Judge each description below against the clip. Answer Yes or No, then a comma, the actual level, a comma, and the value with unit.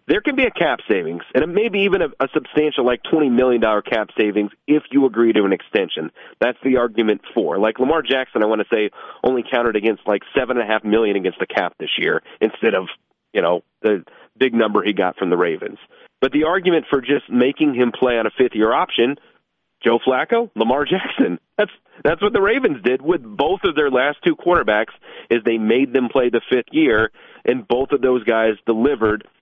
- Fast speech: Yes, fast, 215 wpm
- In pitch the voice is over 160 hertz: No, low, 125 Hz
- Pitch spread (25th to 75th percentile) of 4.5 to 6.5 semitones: Yes, average, 5.0 semitones